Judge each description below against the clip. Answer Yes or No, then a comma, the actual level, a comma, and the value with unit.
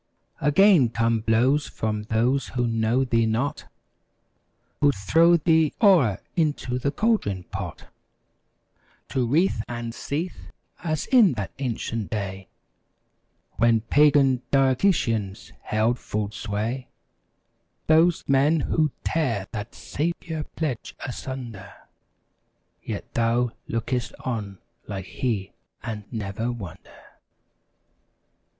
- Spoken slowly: Yes, slow, 105 wpm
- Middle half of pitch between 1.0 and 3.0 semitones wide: No, average, 5.0 semitones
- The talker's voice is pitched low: Yes, low, 120 Hz